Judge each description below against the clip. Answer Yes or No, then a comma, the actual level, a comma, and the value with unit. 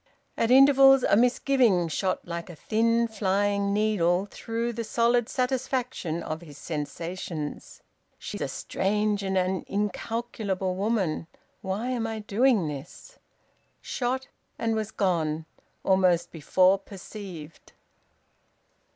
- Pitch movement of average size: Yes, average, 4.5 semitones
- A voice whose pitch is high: Yes, high, 200 Hz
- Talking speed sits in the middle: No, slow, 115 wpm